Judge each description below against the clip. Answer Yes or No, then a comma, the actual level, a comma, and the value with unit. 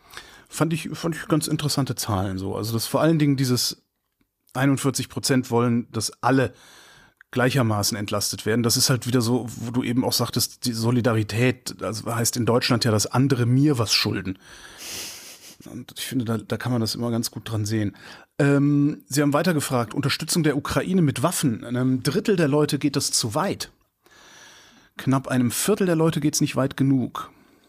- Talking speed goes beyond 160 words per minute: Yes, average, 185 wpm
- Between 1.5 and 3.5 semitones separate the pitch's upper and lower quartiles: No, average, 3.9 semitones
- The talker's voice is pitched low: Yes, low, 125 Hz